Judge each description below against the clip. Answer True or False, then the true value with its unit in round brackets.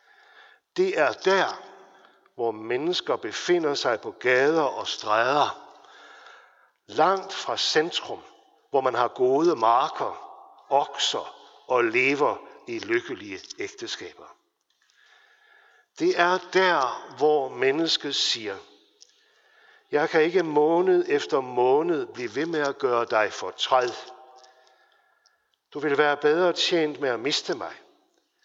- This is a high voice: True (355 Hz)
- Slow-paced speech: True (115 wpm)